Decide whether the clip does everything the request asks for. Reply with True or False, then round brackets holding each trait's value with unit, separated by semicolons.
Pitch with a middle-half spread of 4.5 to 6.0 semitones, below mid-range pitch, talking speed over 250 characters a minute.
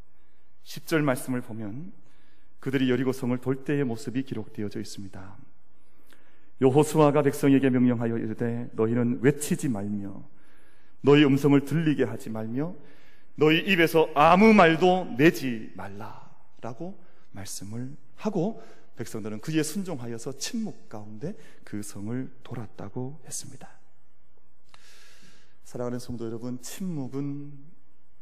True (5.3 semitones; 130 Hz; 265 characters per minute)